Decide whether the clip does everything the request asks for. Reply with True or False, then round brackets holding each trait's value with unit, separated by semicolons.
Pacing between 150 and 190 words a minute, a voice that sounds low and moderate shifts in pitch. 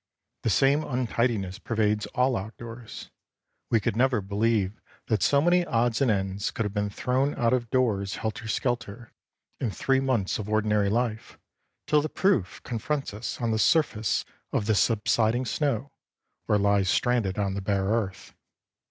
True (160 wpm; 115 Hz; 3.5 semitones)